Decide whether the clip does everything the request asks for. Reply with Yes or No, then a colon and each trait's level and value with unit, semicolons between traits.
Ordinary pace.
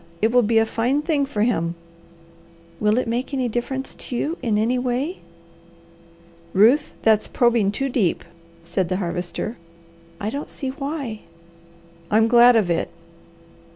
Yes: average, 150 wpm